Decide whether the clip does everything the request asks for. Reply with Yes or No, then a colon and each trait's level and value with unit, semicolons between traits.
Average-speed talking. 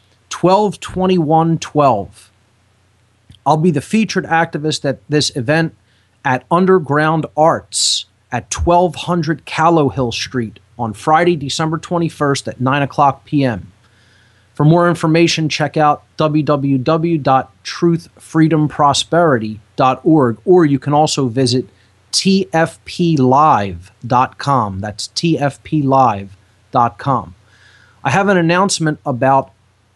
No: slow, 95 wpm